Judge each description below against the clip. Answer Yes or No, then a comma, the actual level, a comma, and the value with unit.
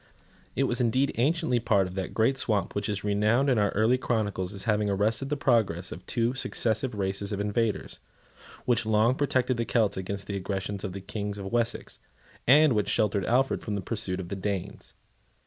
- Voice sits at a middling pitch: No, low, 105 Hz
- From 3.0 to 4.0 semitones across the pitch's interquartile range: Yes, average, 3.3 semitones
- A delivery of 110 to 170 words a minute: No, average, 195 wpm